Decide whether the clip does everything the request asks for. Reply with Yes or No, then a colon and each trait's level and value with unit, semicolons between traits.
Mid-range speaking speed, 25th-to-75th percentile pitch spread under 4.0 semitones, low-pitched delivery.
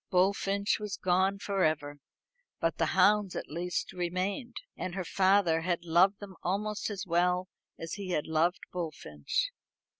No: average, 150 wpm; narrow, 2.6 semitones; medium, 185 Hz